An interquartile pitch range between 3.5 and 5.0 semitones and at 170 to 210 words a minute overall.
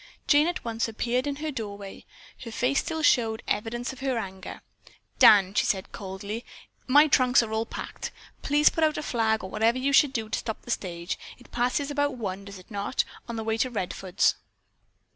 Yes: average, 4.6 semitones; average, 200 wpm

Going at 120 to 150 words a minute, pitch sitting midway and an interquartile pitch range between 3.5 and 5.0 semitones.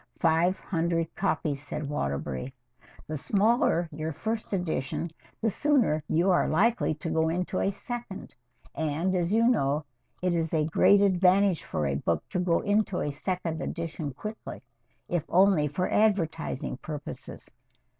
Yes: average, 145 wpm; medium, 170 Hz; average, 4.3 semitones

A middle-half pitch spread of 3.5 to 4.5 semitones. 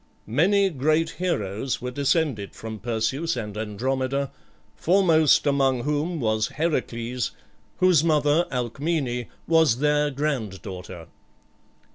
No: average, 5.2 semitones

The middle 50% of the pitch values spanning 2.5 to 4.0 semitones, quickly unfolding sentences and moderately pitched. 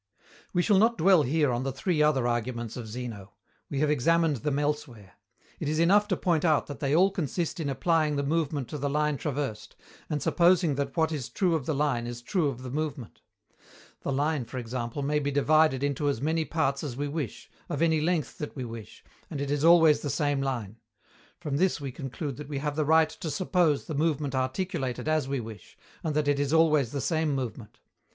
Yes: average, 3.2 semitones; fast, 215 wpm; medium, 145 Hz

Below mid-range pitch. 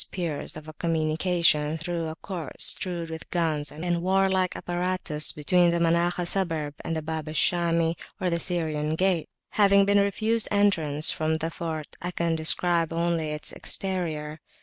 No: medium, 170 Hz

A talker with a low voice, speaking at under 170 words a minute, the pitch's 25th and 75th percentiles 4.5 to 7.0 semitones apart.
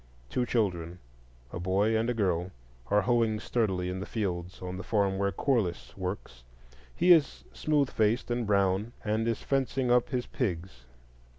Yes: low, 100 Hz; average, 155 wpm; average, 4.8 semitones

